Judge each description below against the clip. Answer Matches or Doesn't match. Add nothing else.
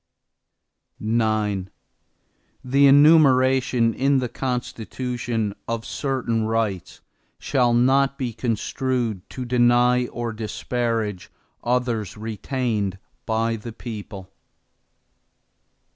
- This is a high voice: Doesn't match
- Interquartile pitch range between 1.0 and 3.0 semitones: Matches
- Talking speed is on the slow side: Matches